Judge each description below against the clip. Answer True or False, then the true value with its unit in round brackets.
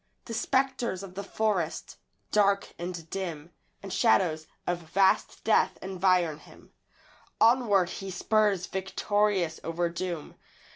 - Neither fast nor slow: False (115 wpm)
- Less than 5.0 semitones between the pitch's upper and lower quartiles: True (3.0 semitones)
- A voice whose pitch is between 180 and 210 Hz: True (190 Hz)